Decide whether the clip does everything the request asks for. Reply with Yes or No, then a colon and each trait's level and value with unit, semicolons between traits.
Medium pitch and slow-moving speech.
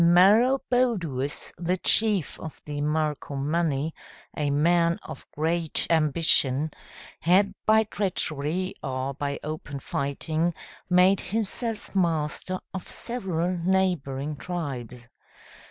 Yes: medium, 165 Hz; slow, 95 wpm